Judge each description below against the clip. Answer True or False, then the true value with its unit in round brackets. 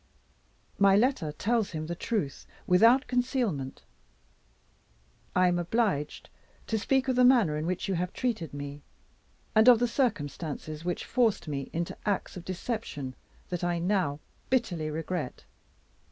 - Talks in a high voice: False (180 Hz)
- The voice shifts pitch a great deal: True (7.0 semitones)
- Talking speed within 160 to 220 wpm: False (140 wpm)